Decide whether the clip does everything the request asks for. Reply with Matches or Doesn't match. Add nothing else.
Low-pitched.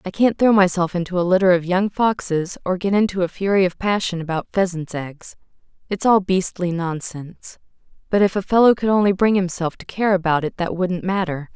Doesn't match